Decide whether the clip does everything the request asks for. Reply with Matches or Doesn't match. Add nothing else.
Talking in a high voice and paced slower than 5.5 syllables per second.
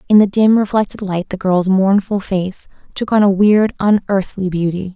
Matches